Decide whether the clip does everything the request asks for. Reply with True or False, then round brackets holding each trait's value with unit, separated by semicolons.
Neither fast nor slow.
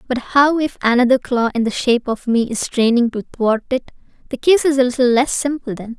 False (220 wpm)